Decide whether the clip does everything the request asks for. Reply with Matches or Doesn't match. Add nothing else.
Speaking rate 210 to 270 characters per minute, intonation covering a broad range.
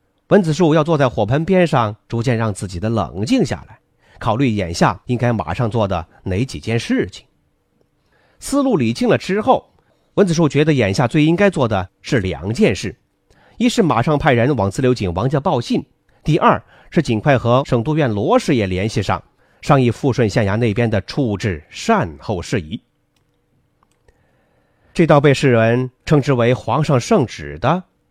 Matches